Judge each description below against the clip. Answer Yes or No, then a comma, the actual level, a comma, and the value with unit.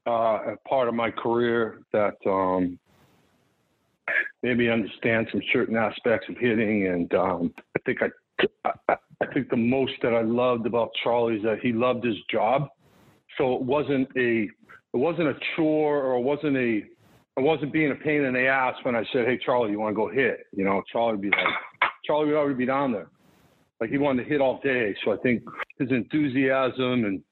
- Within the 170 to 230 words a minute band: Yes, average, 200 wpm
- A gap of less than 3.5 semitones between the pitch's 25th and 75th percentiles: Yes, average, 3.0 semitones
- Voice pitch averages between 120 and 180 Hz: Yes, low, 125 Hz